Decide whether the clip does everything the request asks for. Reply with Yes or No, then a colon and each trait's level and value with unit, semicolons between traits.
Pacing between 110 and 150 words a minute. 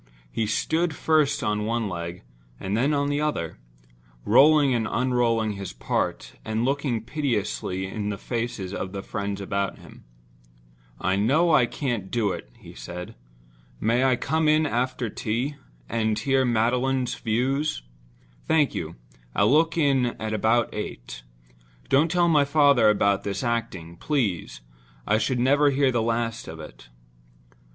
Yes: average, 145 wpm